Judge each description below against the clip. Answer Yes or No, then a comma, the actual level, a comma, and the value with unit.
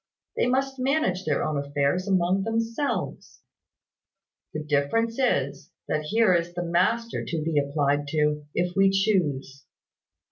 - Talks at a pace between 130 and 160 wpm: Yes, slow, 135 wpm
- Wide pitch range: Yes, wide, 7.3 semitones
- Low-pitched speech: No, medium, 175 Hz